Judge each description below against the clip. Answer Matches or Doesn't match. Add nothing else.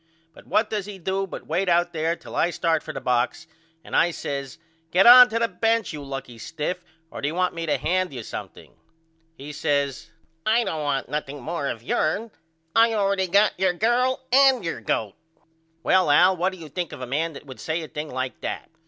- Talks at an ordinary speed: Doesn't match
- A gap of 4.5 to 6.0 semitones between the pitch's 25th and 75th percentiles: Matches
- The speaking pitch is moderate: Matches